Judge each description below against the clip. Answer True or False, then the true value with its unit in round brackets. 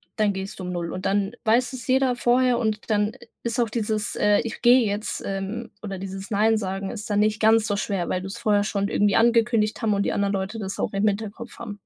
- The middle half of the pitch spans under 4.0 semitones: True (2.6 semitones)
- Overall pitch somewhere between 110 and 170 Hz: False (210 Hz)